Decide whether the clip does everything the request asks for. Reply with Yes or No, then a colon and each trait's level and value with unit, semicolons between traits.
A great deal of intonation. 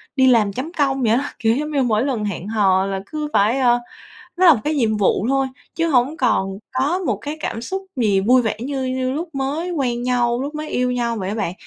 No: average, 4.4 semitones